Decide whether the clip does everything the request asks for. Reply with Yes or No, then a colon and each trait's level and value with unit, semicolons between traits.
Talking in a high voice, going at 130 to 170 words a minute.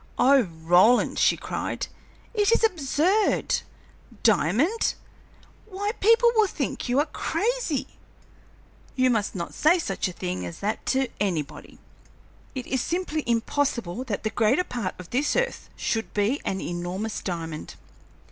Yes: very high, 250 Hz; average, 140 wpm